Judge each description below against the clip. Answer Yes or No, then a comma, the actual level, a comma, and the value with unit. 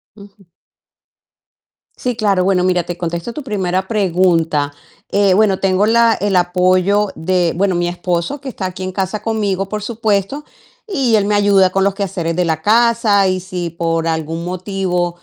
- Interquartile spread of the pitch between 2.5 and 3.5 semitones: Yes, average, 2.8 semitones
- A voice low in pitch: No, high, 190 Hz